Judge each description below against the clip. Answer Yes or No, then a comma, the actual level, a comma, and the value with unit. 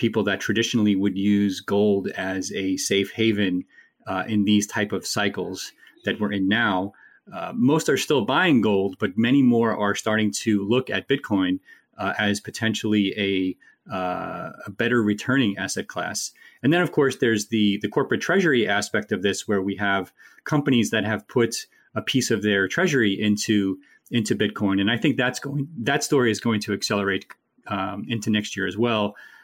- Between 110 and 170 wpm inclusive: No, average, 180 wpm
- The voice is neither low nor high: No, low, 105 Hz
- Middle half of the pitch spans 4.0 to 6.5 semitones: No, narrow, 2.5 semitones